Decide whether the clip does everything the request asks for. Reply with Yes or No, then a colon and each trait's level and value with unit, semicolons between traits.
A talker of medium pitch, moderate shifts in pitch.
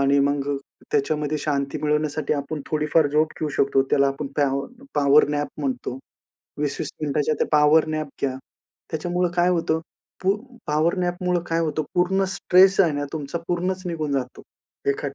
Yes: medium, 150 Hz; average, 3.1 semitones